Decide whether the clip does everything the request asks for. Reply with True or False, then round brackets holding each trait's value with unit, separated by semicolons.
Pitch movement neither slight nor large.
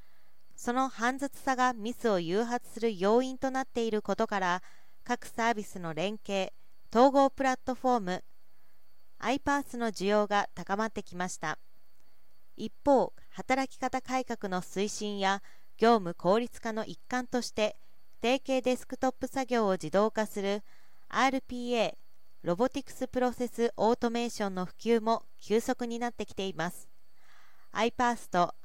True (4.0 semitones)